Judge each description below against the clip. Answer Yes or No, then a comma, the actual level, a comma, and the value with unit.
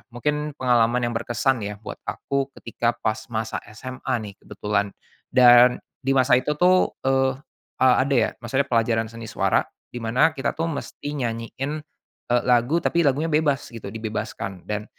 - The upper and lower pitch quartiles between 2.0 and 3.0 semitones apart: No, average, 3.5 semitones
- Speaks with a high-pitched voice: No, low, 125 Hz